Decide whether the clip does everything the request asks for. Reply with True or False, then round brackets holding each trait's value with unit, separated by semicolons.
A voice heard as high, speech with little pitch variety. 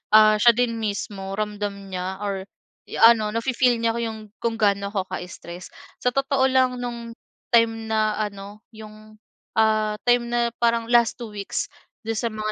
True (220 Hz; 2.2 semitones)